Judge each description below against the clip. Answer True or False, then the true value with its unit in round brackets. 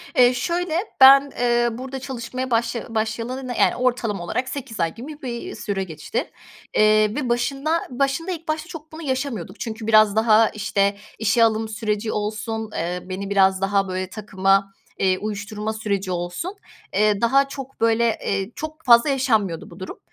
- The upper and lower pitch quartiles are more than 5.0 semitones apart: False (4.4 semitones)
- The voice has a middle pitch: False (225 Hz)